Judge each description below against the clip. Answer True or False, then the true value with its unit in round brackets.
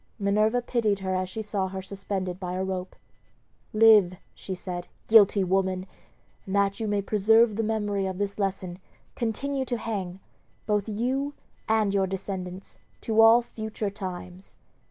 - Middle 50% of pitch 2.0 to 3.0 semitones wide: True (2.7 semitones)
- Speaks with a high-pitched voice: True (200 Hz)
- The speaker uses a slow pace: False (155 wpm)